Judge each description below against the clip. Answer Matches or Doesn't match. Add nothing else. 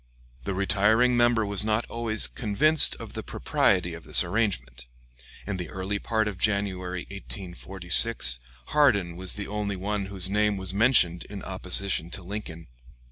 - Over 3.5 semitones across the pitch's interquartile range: Doesn't match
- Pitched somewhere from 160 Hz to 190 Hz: Doesn't match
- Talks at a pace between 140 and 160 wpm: Matches